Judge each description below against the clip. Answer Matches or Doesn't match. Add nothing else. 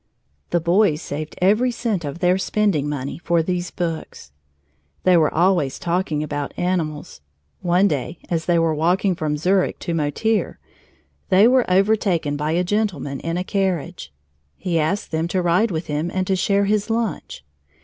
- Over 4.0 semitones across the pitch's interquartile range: Doesn't match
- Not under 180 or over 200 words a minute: Doesn't match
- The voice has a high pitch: Doesn't match